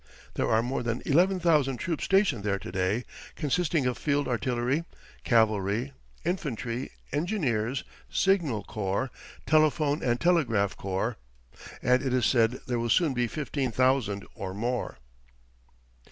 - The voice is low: Yes, low, 125 Hz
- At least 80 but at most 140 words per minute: Yes, slow, 135 wpm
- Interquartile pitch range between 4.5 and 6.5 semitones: Yes, average, 4.9 semitones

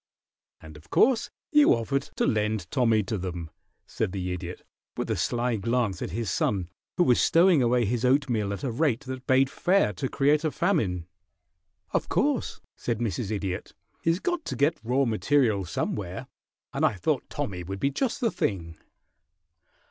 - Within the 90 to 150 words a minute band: No, average, 170 wpm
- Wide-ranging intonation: Yes, wide, 6.2 semitones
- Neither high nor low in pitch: No, low, 115 Hz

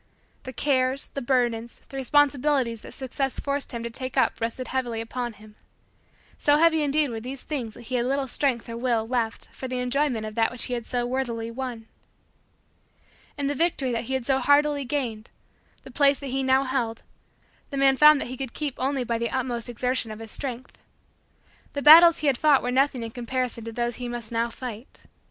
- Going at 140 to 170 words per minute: No, fast, 205 wpm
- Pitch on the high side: Yes, very high, 255 Hz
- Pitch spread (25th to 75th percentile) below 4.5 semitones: Yes, average, 2.8 semitones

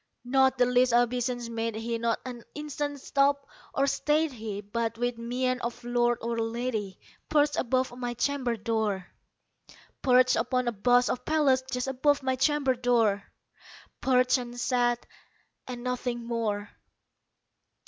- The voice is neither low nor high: No, high, 245 Hz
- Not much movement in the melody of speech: Yes, narrow, 1.9 semitones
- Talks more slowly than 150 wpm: Yes, average, 140 wpm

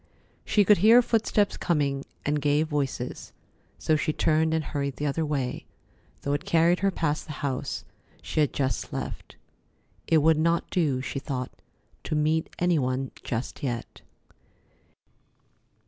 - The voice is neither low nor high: Yes, medium, 150 Hz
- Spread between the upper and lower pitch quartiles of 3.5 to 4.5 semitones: No, average, 3.0 semitones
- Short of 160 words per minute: Yes, average, 145 wpm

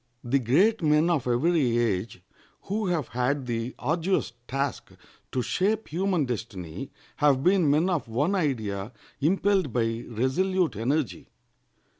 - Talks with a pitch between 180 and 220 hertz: No, medium, 140 Hz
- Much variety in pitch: Yes, wide, 6.6 semitones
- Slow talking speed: Yes, slow, 130 wpm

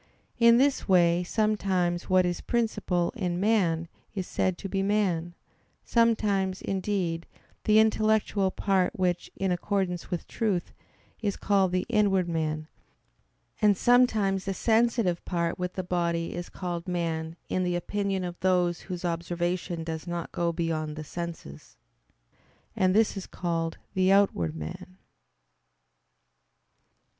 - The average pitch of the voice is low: No, medium, 185 Hz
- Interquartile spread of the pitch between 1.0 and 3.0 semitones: Yes, average, 2.7 semitones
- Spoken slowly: Yes, slow, 130 wpm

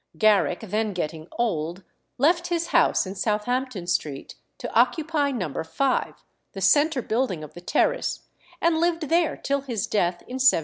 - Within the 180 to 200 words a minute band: No, average, 160 wpm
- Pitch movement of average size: No, wide, 8.1 semitones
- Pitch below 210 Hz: No, high, 230 Hz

